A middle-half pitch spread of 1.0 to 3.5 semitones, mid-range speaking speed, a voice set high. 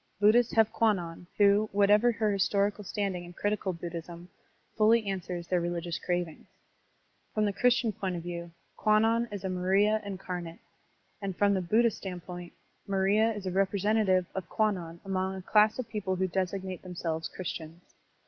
Yes: average, 3.1 semitones; average, 160 wpm; high, 195 Hz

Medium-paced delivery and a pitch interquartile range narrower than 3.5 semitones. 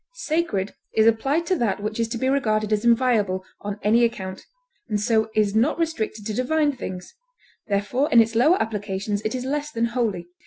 No: average, 190 wpm; average, 3.8 semitones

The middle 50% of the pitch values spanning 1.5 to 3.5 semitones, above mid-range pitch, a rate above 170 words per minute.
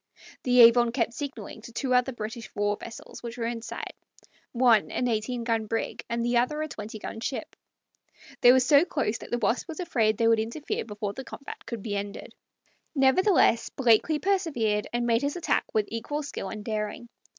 Yes: average, 3.1 semitones; high, 235 Hz; average, 195 wpm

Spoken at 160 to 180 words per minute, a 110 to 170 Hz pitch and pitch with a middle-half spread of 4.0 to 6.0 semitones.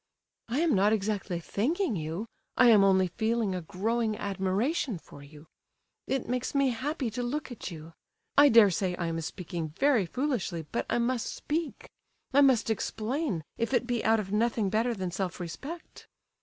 No: average, 170 wpm; high, 220 Hz; average, 5.2 semitones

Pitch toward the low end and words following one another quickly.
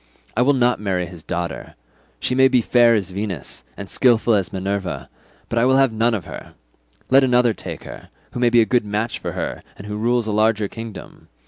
Yes: low, 110 Hz; fast, 215 wpm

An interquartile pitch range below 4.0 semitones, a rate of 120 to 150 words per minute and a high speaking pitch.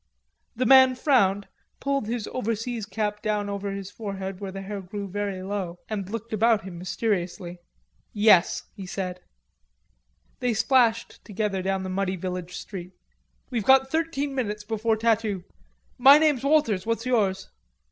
Yes: average, 3.4 semitones; average, 145 wpm; high, 210 Hz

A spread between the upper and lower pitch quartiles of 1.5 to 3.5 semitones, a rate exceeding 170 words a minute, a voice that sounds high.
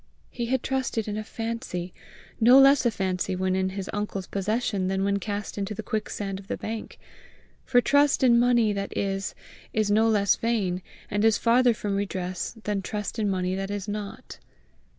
Yes: average, 2.9 semitones; average, 185 wpm; high, 205 Hz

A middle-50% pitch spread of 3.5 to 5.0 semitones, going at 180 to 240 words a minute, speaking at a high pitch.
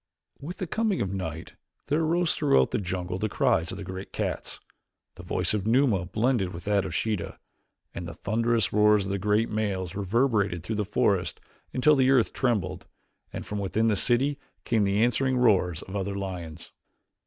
No: average, 4.4 semitones; average, 185 wpm; low, 105 Hz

